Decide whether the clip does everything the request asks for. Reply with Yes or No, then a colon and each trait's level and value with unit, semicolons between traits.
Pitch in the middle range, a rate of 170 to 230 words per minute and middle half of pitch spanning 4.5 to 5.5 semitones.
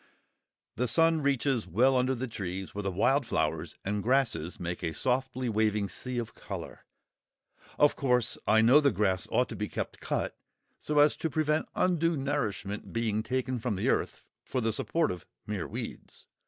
No: low, 125 Hz; average, 175 wpm; average, 5.0 semitones